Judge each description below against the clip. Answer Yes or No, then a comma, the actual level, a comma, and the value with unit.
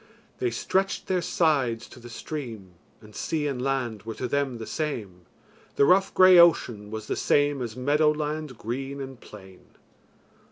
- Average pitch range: Yes, average, 5.0 semitones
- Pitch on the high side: No, low, 135 Hz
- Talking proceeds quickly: No, average, 165 wpm